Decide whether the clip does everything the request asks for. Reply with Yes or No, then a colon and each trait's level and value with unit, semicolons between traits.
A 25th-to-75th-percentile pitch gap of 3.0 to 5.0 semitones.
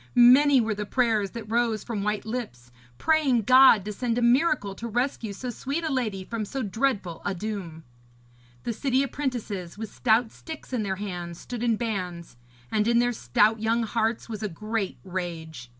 Yes: average, 3.6 semitones